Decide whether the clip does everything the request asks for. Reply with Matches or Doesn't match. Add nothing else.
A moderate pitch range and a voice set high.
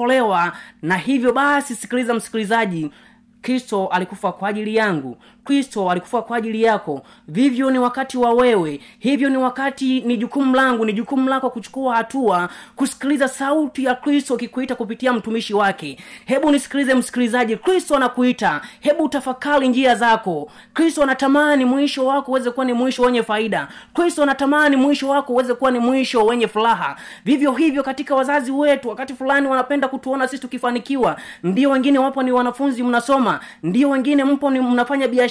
Matches